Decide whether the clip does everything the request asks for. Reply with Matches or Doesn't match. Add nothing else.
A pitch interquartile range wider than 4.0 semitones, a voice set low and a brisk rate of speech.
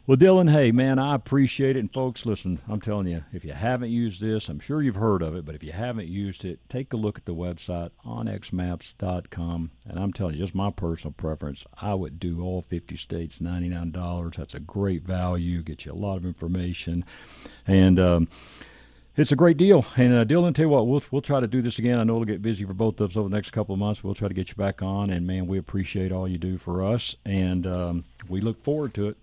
Matches